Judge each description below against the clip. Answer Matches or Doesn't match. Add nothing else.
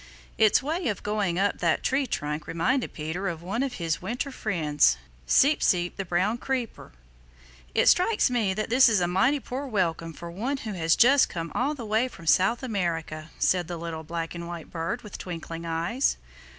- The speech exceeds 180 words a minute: Matches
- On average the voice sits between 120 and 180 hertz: Doesn't match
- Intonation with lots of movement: Matches